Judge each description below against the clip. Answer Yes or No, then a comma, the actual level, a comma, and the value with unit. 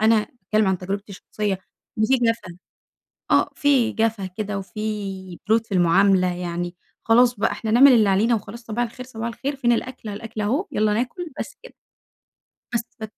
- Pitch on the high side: Yes, high, 215 Hz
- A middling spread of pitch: Yes, average, 3.2 semitones